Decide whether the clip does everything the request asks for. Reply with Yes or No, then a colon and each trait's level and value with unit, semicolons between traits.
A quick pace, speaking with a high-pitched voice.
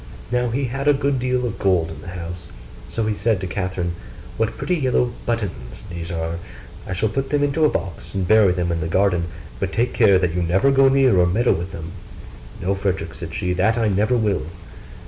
No: fast, 220 wpm; low, 100 Hz